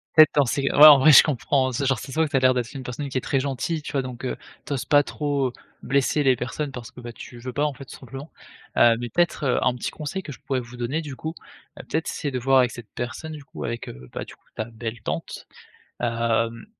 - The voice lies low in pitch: Yes, low, 130 Hz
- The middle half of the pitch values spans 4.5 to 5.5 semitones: No, average, 3.1 semitones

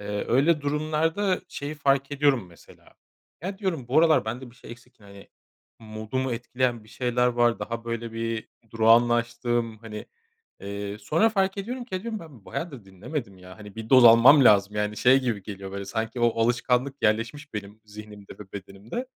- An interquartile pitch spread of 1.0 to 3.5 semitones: No, average, 4.8 semitones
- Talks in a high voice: No, low, 120 Hz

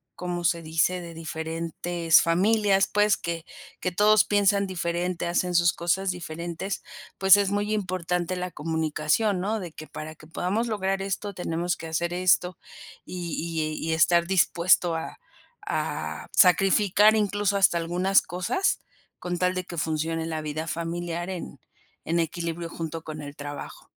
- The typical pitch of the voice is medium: Yes, medium, 175 Hz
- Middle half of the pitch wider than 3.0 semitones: No, average, 2.7 semitones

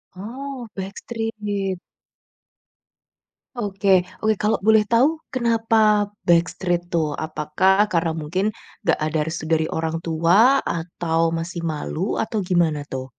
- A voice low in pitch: No, medium, 180 Hz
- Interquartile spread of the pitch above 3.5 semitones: Yes, average, 4.8 semitones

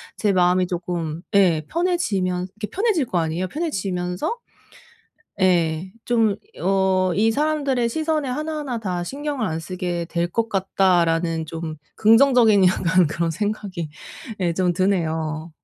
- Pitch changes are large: No, average, 5.0 semitones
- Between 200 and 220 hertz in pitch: No, medium, 185 Hz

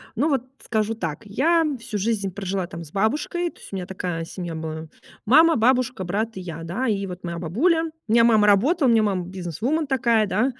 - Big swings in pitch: Yes, wide, 5.8 semitones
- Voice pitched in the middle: No, high, 210 Hz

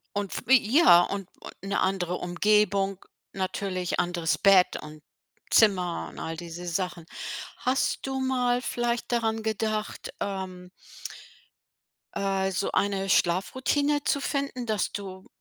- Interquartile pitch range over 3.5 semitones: Yes, average, 4.5 semitones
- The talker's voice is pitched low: No, high, 195 Hz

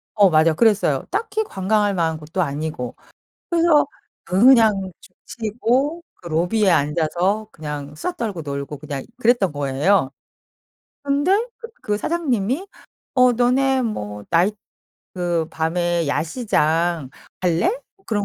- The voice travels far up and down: Yes, wide, 7.5 semitones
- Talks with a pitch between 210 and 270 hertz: No, high, 190 Hz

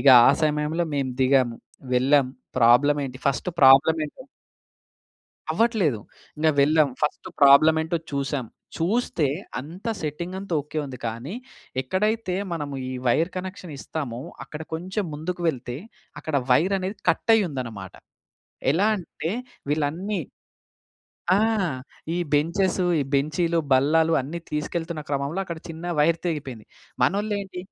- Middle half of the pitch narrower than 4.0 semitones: No, average, 4.3 semitones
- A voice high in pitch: No, medium, 155 Hz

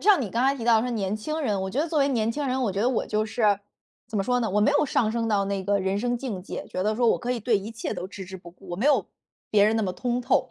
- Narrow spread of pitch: No, average, 3.7 semitones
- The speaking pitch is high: Yes, high, 220 Hz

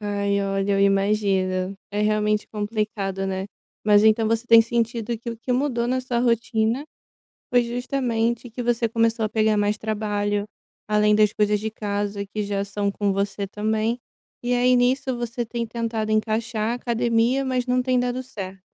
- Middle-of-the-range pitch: No, high, 220 Hz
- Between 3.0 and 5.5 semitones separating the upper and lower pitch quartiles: No, narrow, 2.6 semitones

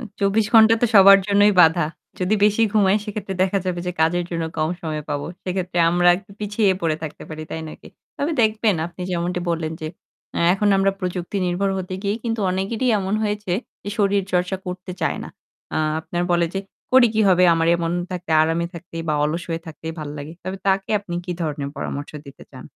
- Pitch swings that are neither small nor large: Yes, average, 3.3 semitones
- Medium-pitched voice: Yes, medium, 180 Hz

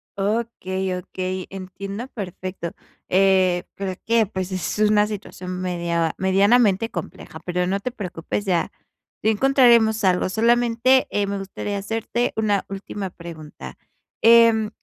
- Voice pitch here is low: No, high, 195 Hz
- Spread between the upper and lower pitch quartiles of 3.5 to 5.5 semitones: No, average, 3.1 semitones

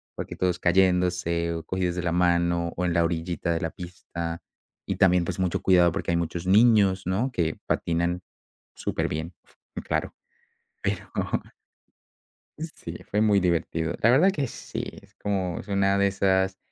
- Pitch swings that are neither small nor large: No, narrow, 2.1 semitones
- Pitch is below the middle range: Yes, very low, 90 Hz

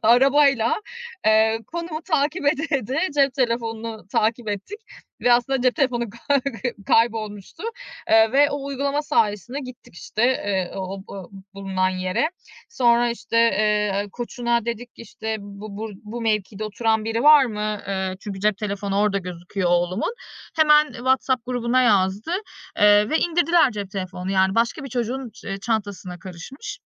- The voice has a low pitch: No, high, 225 Hz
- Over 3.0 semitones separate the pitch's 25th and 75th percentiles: Yes, average, 4.5 semitones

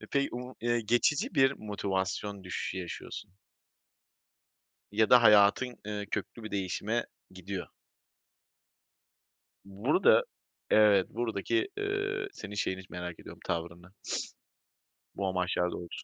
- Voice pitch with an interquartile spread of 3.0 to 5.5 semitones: Yes, average, 4.4 semitones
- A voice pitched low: Yes, low, 105 Hz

